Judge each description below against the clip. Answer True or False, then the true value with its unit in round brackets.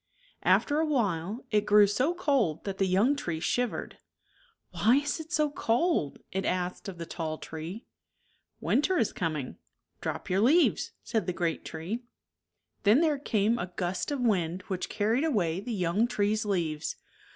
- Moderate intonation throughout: False (6.6 semitones)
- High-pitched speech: True (210 Hz)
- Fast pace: False (175 wpm)